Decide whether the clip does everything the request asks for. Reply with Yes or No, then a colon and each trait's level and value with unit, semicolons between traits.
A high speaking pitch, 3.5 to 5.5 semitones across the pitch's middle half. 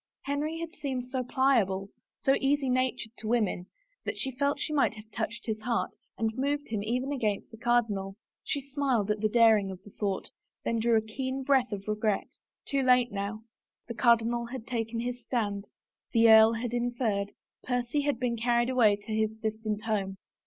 No: high, 235 Hz; average, 3.1 semitones